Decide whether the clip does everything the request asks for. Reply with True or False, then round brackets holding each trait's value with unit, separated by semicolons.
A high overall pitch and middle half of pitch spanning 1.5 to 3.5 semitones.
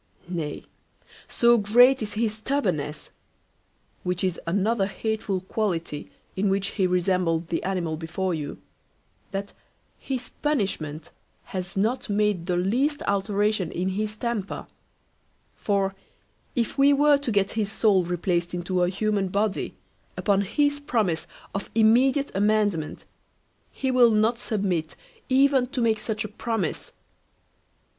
False (200 Hz; 4.0 semitones)